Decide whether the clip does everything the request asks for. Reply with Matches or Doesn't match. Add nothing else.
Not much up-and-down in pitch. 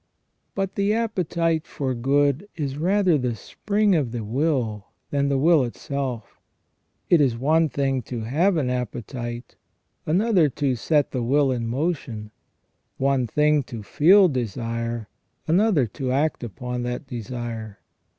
Doesn't match